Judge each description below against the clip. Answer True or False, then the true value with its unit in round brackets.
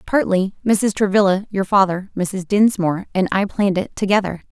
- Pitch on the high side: True (195 Hz)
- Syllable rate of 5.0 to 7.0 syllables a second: True (5.2 syllables/s)